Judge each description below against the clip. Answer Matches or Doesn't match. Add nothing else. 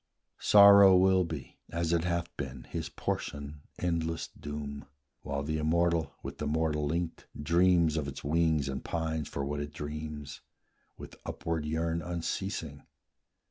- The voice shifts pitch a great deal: Doesn't match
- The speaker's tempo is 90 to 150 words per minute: Matches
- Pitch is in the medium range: Doesn't match